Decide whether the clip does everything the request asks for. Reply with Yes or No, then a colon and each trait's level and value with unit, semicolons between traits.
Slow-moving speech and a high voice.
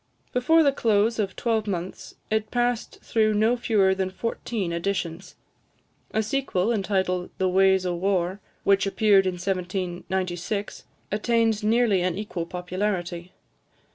Yes: slow, 125 wpm; high, 195 Hz